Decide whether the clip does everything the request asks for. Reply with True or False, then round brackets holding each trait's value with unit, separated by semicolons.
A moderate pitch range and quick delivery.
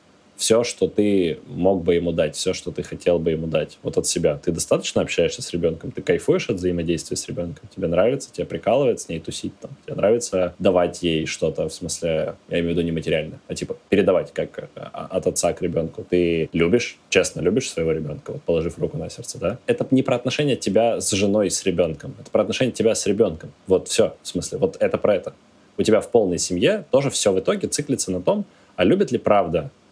False (8.1 semitones; 215 wpm)